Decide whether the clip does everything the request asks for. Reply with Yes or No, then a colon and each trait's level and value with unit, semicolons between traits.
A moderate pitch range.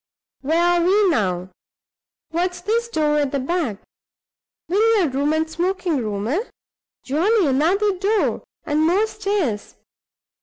No: wide, 5.7 semitones